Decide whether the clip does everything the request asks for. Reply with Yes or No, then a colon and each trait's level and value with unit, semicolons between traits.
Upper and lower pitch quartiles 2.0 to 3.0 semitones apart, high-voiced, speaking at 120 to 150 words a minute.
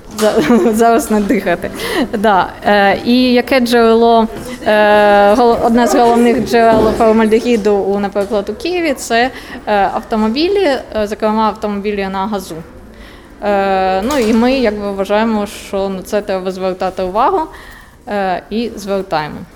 Yes: average, 2.7 semitones; high, 215 Hz; average, 125 wpm